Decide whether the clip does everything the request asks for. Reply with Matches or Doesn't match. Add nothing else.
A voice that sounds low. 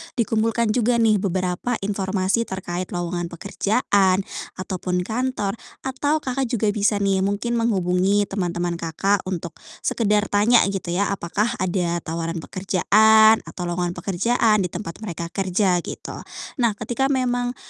Doesn't match